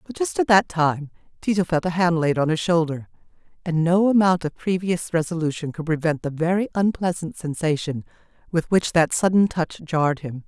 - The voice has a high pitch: No, medium, 170 Hz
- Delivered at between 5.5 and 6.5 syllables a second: No, 5.2 syllables/s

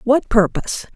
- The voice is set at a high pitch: Yes, high, 235 Hz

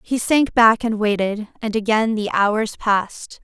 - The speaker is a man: No, female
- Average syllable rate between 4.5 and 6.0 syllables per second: No, 4.1 syllables/s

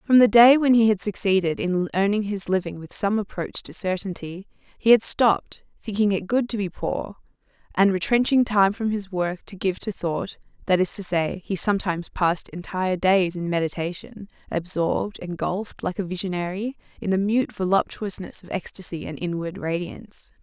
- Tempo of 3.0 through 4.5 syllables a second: No, 5.1 syllables/s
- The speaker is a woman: Yes, female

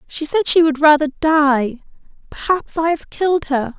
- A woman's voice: Yes, female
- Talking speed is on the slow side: No, average, 175 wpm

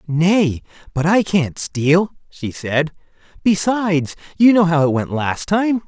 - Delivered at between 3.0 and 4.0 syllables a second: Yes, 3.8 syllables/s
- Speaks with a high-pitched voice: No, medium, 170 Hz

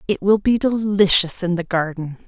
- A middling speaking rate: Yes, average, 185 wpm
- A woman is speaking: Yes, female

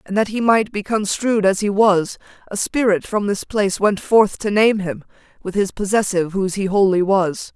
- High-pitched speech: Yes, high, 200 Hz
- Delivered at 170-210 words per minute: Yes, fast, 205 wpm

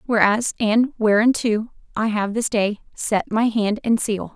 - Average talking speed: Yes, average, 165 wpm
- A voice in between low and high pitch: No, high, 220 Hz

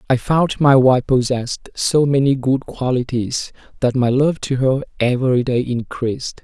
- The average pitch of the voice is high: No, low, 130 Hz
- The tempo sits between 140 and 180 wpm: Yes, average, 160 wpm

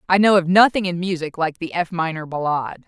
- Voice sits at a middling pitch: Yes, medium, 175 Hz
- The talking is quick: Yes, fast, 230 wpm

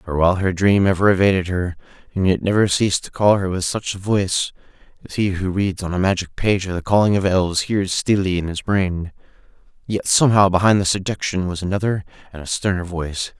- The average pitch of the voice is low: Yes, very low, 95 Hz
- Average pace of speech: No, fast, 210 wpm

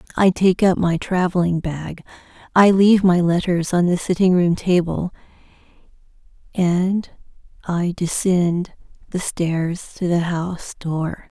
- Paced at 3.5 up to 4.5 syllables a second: Yes, 4.0 syllables/s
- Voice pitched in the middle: Yes, medium, 175 Hz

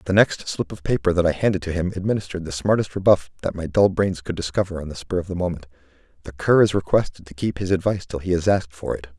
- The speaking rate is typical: No, fast, 260 wpm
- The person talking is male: Yes, male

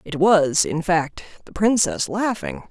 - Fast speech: No, average, 155 wpm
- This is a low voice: No, medium, 185 Hz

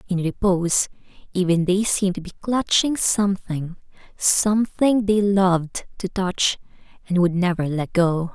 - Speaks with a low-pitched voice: No, medium, 185 Hz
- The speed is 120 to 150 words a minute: Yes, slow, 135 wpm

